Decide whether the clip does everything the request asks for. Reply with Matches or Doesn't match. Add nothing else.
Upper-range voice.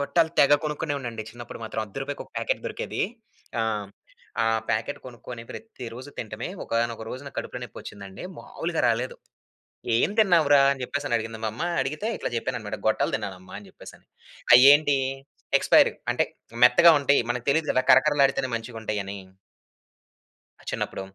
Doesn't match